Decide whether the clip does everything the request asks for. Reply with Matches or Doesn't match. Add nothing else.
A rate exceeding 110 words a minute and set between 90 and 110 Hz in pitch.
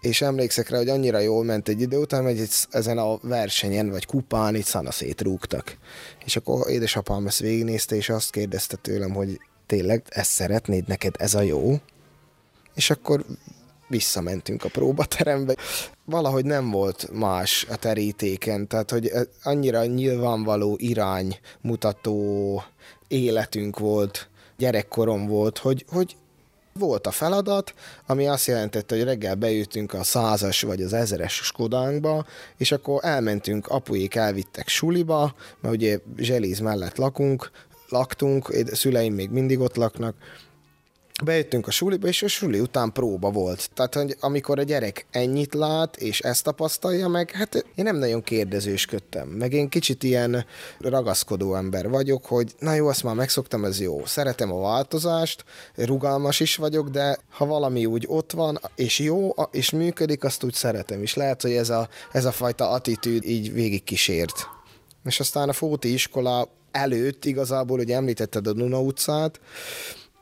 Doesn't match